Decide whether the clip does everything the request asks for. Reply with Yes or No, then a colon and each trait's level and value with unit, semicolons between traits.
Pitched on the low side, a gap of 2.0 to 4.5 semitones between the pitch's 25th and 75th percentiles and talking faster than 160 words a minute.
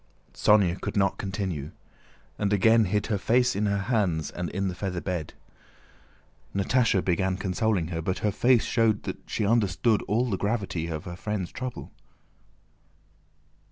No: low, 100 Hz; average, 3.2 semitones; average, 155 wpm